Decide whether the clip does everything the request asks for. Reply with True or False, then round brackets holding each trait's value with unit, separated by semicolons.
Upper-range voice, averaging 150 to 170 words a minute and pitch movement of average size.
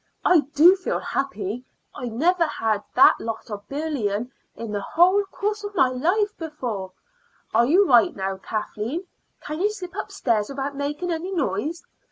False (280 Hz; 165 wpm; 8.1 semitones)